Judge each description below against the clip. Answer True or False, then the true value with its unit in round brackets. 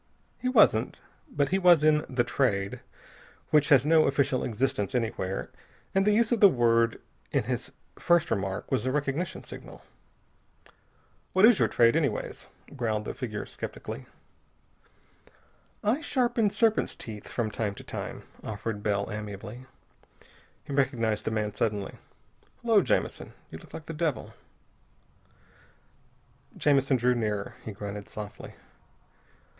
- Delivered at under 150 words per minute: True (135 wpm)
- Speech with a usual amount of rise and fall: False (6.8 semitones)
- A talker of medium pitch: False (125 Hz)